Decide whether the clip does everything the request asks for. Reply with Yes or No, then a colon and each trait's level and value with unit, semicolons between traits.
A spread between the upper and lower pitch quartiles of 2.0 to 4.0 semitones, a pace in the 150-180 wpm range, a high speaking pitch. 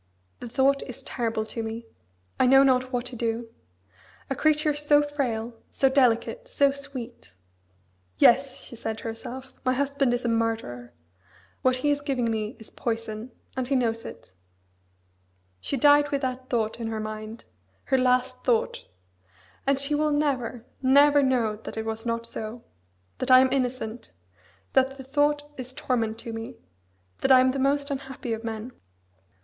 Yes: average, 3.3 semitones; average, 165 wpm; very high, 255 Hz